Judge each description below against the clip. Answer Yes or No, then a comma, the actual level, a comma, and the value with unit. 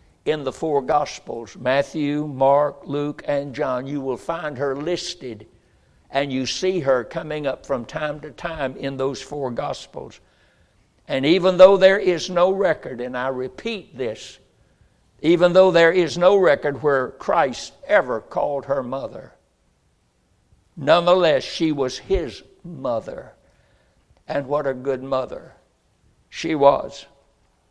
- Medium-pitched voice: Yes, medium, 145 Hz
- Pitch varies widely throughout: No, average, 4.0 semitones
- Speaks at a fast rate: No, slow, 135 wpm